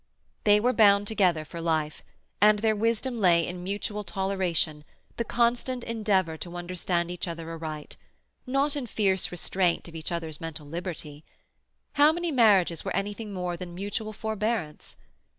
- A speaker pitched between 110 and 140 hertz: No, high, 190 Hz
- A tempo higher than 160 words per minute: No, average, 150 wpm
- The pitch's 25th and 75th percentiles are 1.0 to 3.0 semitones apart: No, average, 4.4 semitones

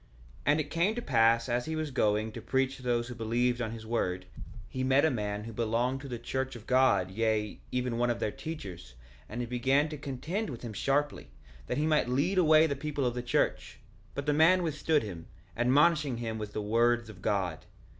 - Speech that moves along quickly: Yes, fast, 220 wpm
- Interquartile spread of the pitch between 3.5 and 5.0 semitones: Yes, average, 4.4 semitones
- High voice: No, low, 125 Hz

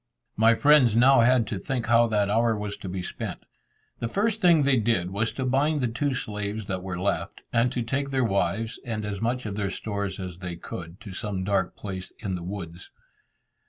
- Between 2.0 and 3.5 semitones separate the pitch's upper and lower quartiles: No, average, 4.3 semitones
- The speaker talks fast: Yes, fast, 210 wpm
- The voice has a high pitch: No, low, 110 Hz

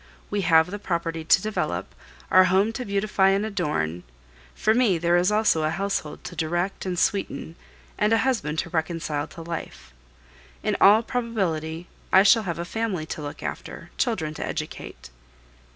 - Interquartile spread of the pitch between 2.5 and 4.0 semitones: No, average, 4.5 semitones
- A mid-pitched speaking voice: Yes, medium, 180 Hz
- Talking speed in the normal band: Yes, average, 170 wpm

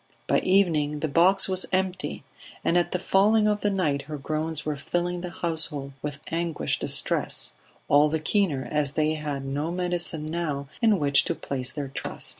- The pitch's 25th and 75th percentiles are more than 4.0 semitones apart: No, average, 3.6 semitones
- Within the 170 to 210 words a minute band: Yes, average, 180 wpm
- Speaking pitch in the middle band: Yes, medium, 160 Hz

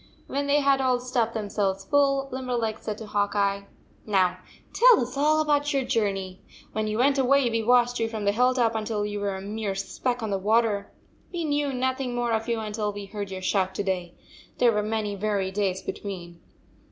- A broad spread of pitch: No, average, 3.9 semitones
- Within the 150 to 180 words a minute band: No, fast, 205 wpm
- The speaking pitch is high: Yes, high, 220 Hz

